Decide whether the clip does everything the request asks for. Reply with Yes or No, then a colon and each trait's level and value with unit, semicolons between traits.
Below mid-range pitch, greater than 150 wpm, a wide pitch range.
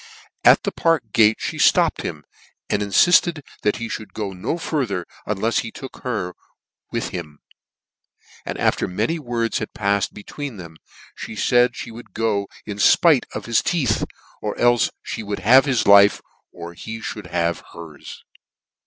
No: low, 110 Hz; average, 170 wpm; average, 3.4 semitones